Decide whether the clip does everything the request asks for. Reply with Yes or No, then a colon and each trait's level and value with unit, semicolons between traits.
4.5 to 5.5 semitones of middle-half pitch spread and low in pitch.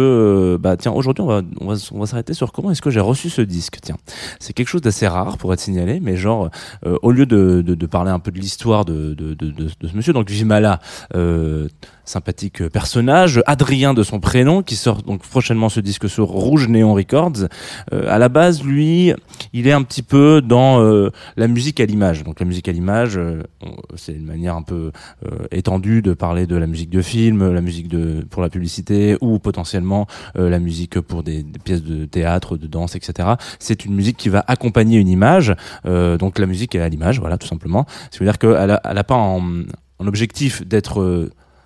Yes: average, 4.8 semitones; low, 100 Hz